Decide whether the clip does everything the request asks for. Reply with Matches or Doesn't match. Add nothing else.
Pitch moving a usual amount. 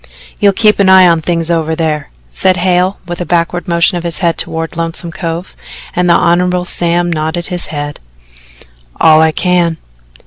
Doesn't match